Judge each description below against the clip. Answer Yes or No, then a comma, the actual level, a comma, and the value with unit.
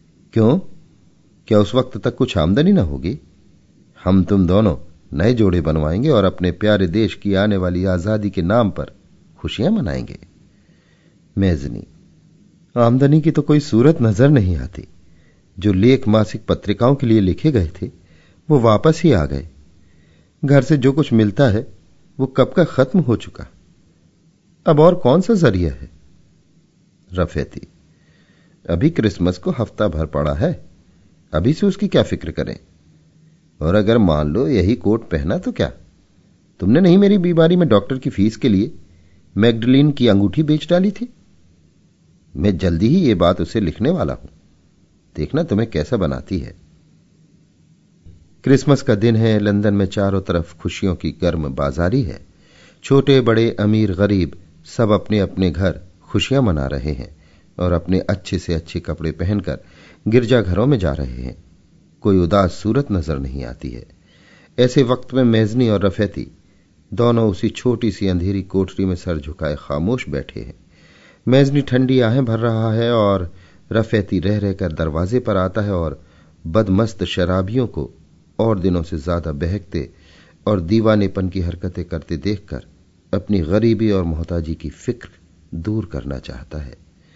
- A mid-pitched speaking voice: No, low, 100 Hz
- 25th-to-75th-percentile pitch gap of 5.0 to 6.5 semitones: Yes, wide, 5.5 semitones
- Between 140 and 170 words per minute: Yes, average, 155 wpm